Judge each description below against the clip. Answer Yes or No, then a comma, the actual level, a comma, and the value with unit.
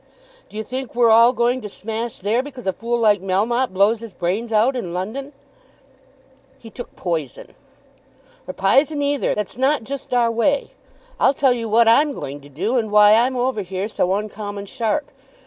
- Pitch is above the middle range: Yes, high, 230 Hz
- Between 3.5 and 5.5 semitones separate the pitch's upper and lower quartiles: Yes, average, 3.8 semitones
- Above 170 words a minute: Yes, average, 180 wpm